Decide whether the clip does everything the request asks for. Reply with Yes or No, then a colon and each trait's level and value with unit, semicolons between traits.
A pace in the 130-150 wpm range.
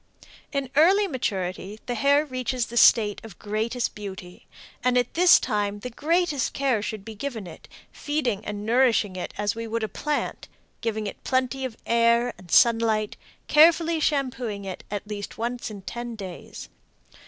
No: average, 160 wpm